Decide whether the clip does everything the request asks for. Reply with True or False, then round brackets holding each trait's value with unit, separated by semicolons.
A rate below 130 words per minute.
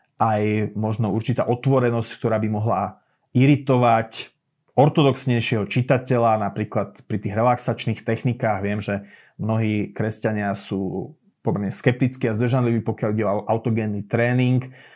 True (115 wpm)